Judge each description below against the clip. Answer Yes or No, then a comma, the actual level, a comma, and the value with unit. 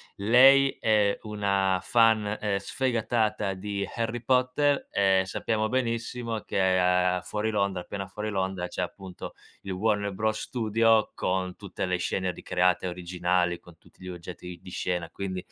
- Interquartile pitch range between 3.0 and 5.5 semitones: Yes, average, 3.3 semitones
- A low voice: Yes, low, 100 Hz